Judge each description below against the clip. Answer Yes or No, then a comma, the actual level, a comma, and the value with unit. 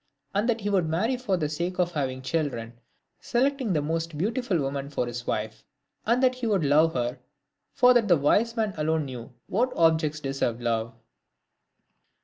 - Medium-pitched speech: Yes, medium, 160 Hz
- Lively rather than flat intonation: Yes, wide, 7.9 semitones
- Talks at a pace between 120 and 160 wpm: No, average, 175 wpm